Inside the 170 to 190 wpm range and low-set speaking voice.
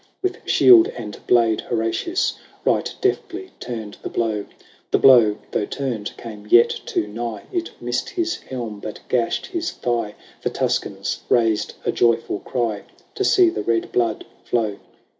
No: average, 150 wpm; low, 120 Hz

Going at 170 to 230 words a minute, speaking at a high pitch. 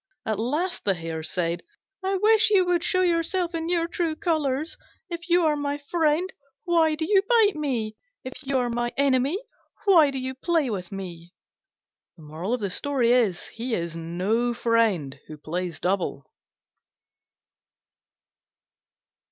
No: slow, 135 wpm; very high, 265 Hz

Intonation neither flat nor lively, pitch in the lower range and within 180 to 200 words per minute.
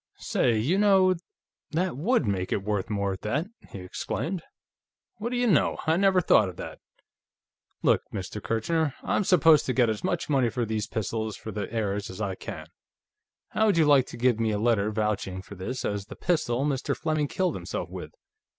No: wide, 7.7 semitones; low, 120 Hz; average, 195 wpm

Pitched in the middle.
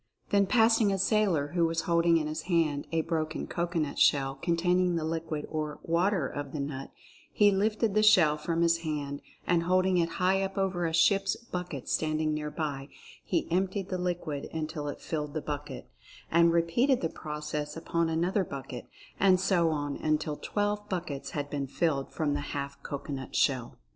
Yes: medium, 165 Hz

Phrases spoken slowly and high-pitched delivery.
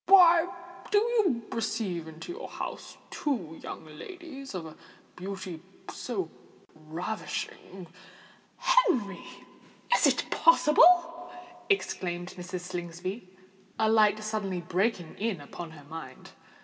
Yes: slow, 110 wpm; high, 200 Hz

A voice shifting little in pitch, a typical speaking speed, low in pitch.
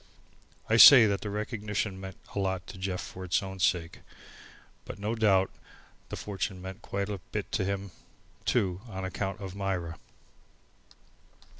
Yes: narrow, 1.5 semitones; average, 155 wpm; very low, 95 Hz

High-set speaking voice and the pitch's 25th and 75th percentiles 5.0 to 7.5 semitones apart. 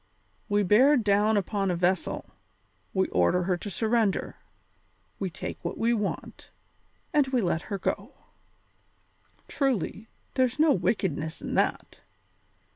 No: high, 205 Hz; average, 4.2 semitones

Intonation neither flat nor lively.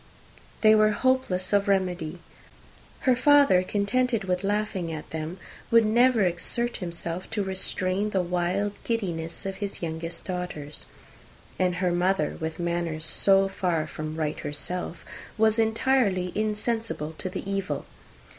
Yes: average, 3.8 semitones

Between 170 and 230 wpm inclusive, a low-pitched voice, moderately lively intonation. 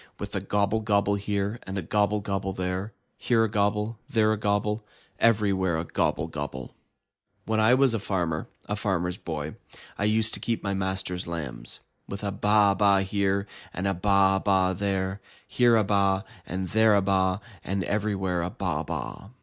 No: average, 175 wpm; low, 100 Hz; narrow, 1.9 semitones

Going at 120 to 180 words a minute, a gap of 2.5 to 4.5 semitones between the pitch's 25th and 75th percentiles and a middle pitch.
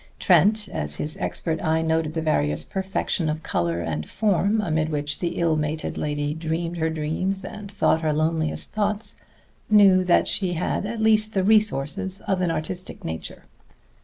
Yes: average, 165 wpm; average, 4.1 semitones; medium, 165 Hz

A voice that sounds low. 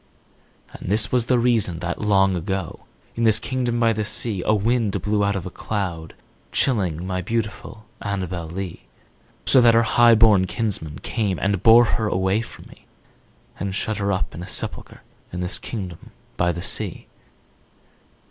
Yes: low, 100 Hz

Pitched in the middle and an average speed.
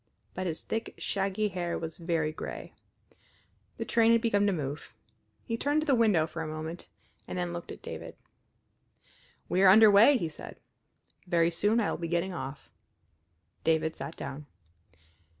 Yes: medium, 175 Hz; average, 170 wpm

